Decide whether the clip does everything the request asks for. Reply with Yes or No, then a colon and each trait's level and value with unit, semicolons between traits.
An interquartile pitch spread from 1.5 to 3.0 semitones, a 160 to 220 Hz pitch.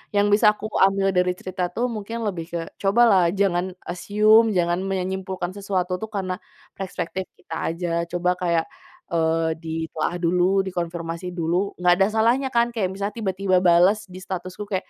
Yes: narrow, 2.5 semitones; medium, 185 Hz